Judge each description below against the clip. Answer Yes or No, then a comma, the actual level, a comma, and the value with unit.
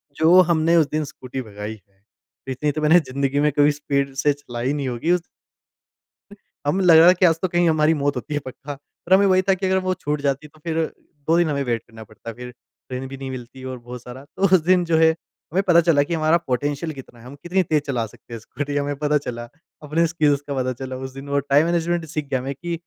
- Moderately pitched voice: Yes, medium, 145 Hz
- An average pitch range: Yes, average, 3.9 semitones